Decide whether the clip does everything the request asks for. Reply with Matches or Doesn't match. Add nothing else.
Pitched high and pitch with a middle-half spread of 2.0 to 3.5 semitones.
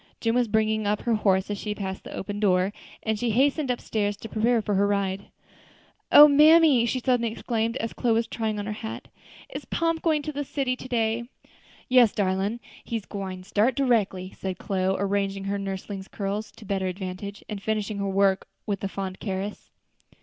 Matches